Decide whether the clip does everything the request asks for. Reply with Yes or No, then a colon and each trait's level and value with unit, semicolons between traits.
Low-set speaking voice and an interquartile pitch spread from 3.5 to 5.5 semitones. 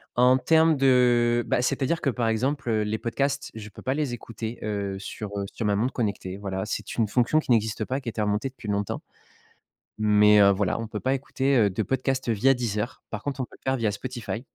Yes: low, 115 Hz; average, 3.9 semitones